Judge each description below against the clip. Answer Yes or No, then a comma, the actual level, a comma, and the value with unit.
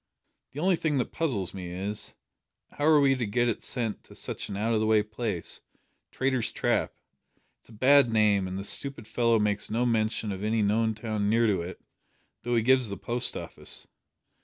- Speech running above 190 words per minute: Yes, average, 200 wpm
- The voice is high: No, low, 110 Hz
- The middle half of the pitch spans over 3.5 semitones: No, average, 3.0 semitones